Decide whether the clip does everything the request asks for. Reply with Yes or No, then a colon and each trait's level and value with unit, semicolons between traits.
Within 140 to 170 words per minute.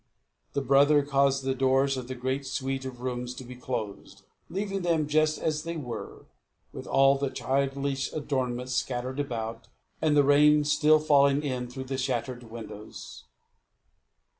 Yes: average, 155 wpm